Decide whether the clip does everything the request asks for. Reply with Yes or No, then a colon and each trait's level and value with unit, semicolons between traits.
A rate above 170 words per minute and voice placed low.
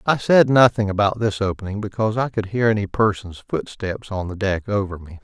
Yes: fast, 205 wpm; low, 105 Hz